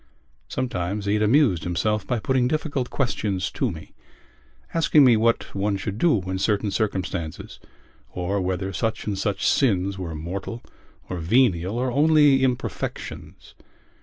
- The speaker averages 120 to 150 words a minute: Yes, average, 140 wpm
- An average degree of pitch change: Yes, average, 4.9 semitones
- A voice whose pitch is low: Yes, low, 105 Hz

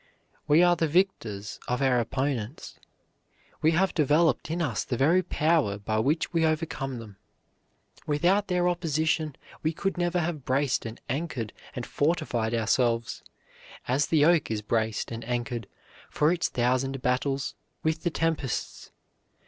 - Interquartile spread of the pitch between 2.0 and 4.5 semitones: No, average, 5.3 semitones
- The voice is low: No, medium, 145 Hz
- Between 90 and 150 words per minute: Yes, average, 145 wpm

